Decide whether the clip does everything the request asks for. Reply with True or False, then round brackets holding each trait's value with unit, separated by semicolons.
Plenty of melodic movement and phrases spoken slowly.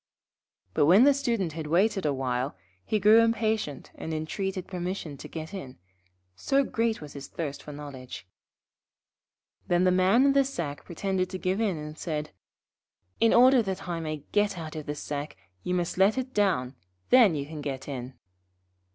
False (5.8 semitones; 175 wpm)